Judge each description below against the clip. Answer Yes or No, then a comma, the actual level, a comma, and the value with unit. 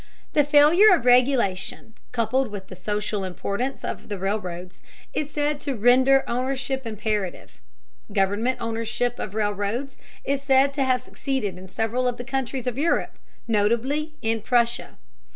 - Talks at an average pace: Yes, average, 145 wpm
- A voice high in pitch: Yes, high, 240 Hz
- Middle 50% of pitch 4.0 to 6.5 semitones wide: Yes, average, 4.3 semitones